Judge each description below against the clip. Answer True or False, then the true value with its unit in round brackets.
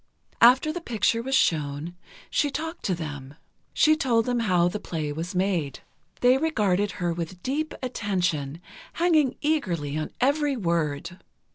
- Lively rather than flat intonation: True (8.2 semitones)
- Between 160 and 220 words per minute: False (145 wpm)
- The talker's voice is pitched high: True (195 Hz)